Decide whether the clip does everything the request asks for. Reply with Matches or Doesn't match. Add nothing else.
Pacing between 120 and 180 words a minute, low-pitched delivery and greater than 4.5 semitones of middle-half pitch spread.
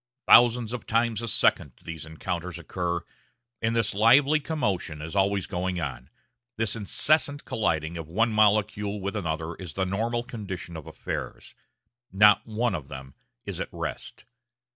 Matches